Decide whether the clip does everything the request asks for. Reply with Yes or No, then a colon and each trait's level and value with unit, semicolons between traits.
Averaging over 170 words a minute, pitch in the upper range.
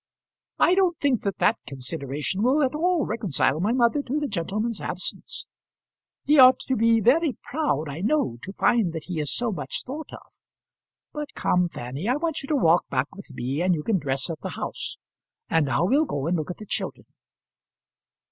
Yes: average, 195 wpm; high, 205 Hz